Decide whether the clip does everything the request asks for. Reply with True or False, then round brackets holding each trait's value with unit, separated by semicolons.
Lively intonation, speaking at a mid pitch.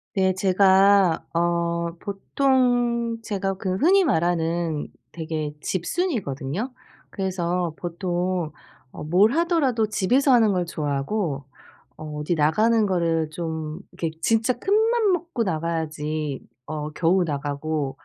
True (5.7 semitones; 180 Hz)